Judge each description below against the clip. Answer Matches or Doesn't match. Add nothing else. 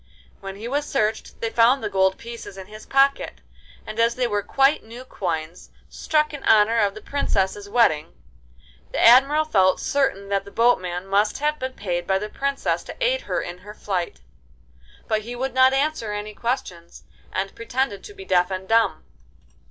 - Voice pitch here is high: Matches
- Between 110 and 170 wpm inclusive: Doesn't match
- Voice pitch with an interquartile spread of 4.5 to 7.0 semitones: Matches